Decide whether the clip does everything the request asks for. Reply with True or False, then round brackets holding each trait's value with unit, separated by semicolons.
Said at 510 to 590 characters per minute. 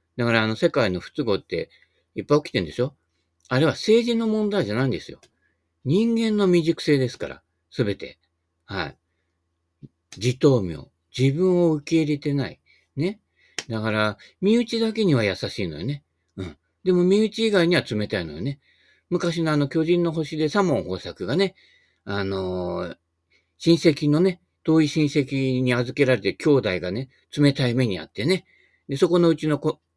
False (310 characters per minute)